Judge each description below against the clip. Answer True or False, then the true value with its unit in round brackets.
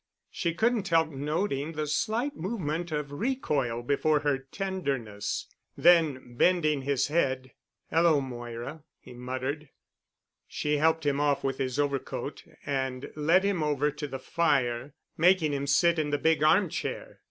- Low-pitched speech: False (150 Hz)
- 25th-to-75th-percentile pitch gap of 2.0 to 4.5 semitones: True (3.6 semitones)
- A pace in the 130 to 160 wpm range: True (145 wpm)